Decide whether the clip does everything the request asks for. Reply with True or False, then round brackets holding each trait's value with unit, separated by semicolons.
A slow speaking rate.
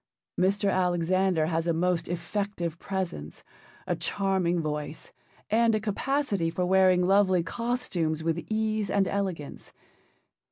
True (120 wpm)